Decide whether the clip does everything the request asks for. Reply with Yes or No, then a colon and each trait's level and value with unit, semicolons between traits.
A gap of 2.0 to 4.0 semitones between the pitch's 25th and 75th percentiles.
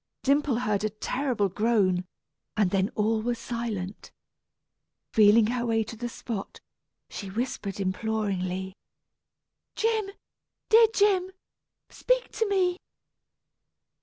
No: average, 5.3 semitones